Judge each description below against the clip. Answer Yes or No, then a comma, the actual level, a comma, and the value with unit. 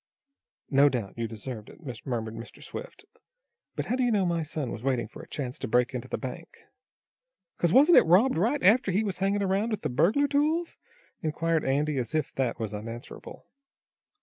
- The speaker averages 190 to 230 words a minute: Yes, average, 200 wpm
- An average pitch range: No, wide, 8.6 semitones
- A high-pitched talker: No, medium, 155 Hz